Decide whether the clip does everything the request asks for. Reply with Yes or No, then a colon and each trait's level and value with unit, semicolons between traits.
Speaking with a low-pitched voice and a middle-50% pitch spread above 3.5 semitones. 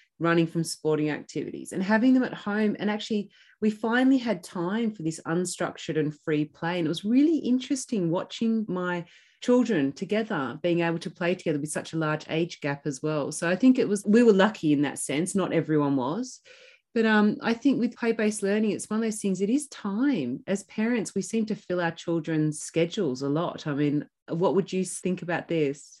No: medium, 185 Hz; average, 5.2 semitones